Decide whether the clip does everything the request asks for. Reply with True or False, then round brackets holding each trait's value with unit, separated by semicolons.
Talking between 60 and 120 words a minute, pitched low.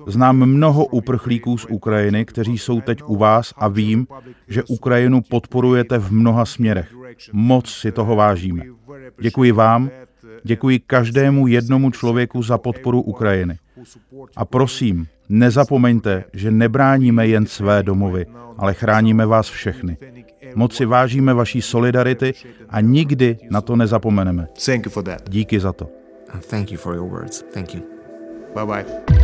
True (115 wpm; 115 Hz)